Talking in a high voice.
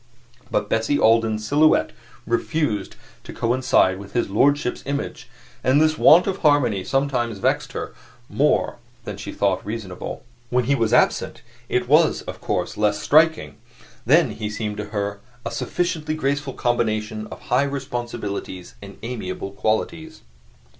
No: low, 120 Hz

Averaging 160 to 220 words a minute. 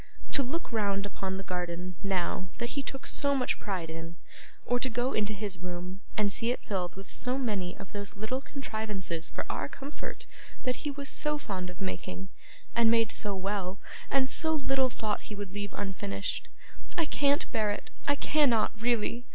Yes: average, 185 wpm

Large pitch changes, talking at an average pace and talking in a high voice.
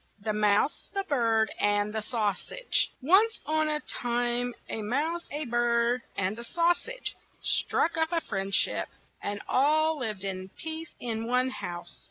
Yes: wide, 6.7 semitones; average, 160 wpm; high, 240 Hz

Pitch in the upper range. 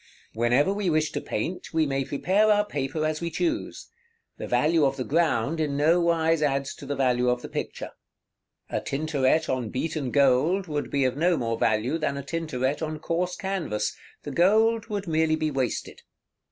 No: medium, 155 Hz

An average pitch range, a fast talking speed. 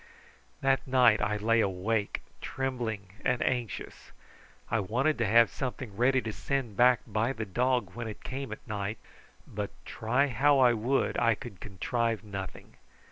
No: average, 3.2 semitones; average, 155 wpm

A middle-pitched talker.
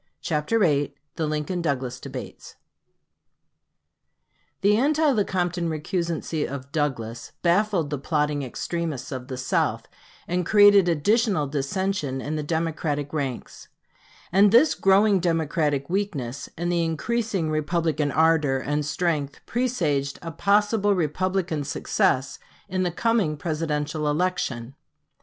Yes: medium, 160 Hz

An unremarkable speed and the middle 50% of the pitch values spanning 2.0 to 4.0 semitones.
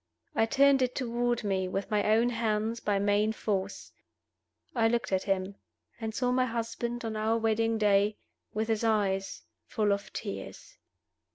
Yes: average, 160 wpm; narrow, 2.4 semitones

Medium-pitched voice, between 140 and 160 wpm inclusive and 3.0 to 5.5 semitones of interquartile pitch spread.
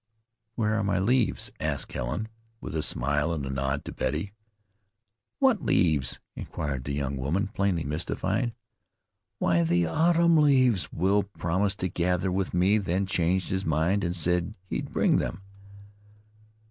No: very low, 90 Hz; average, 145 wpm; average, 4.3 semitones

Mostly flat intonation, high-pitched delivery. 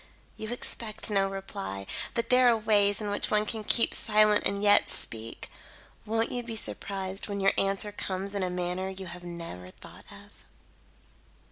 Yes: narrow, 2.3 semitones; high, 200 Hz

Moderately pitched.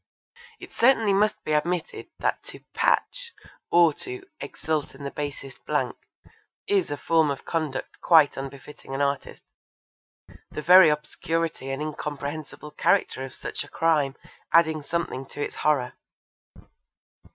Yes: medium, 150 Hz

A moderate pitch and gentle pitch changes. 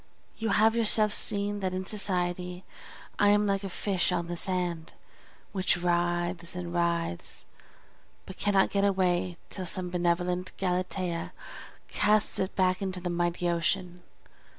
Yes: medium, 180 Hz; narrow, 2.0 semitones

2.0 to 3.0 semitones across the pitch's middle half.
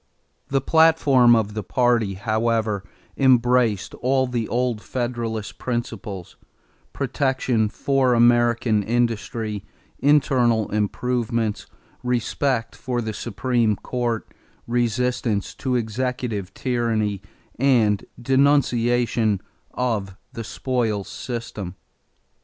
Yes: narrow, 2.5 semitones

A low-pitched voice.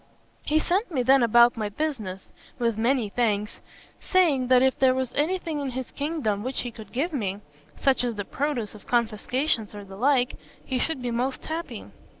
No: very high, 250 Hz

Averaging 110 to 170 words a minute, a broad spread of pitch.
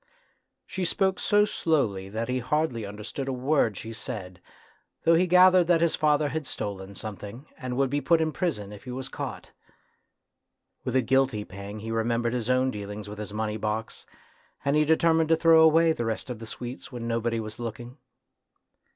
No: average, 185 wpm; wide, 6.2 semitones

